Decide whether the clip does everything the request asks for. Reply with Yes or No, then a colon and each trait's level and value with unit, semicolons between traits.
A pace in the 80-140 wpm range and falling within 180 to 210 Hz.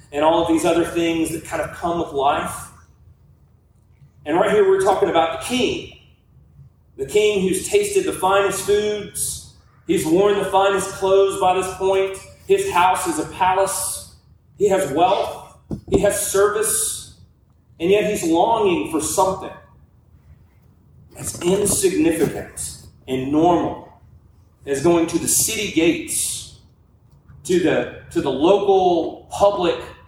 Yes: slow, 135 wpm; high, 190 Hz